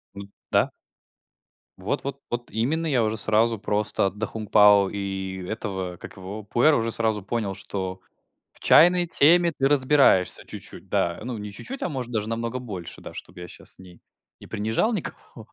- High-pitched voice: No, low, 110 Hz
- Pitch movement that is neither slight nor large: Yes, average, 4.5 semitones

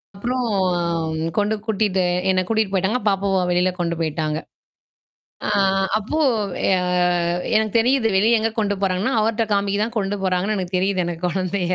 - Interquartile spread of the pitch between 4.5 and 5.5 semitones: No, average, 3.0 semitones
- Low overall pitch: No, high, 200 Hz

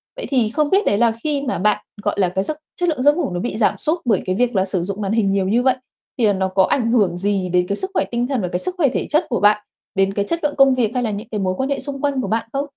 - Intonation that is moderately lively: No, wide, 5.9 semitones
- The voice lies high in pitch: Yes, high, 230 Hz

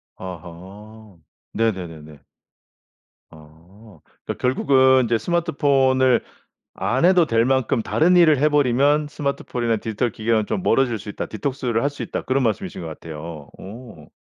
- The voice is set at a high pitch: No, low, 115 Hz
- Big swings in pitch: Yes, wide, 6.1 semitones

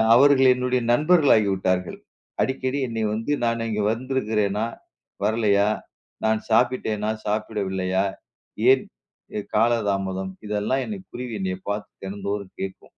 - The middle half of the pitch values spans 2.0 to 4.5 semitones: Yes, average, 3.8 semitones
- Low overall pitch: Yes, low, 110 Hz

